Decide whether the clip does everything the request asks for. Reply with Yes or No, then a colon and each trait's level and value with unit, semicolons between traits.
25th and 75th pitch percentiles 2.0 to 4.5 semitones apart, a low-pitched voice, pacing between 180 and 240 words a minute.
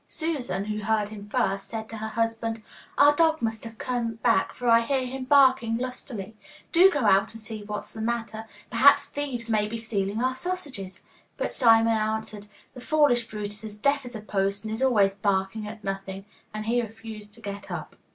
No: average, 3.1 semitones; high, 225 Hz; average, 200 wpm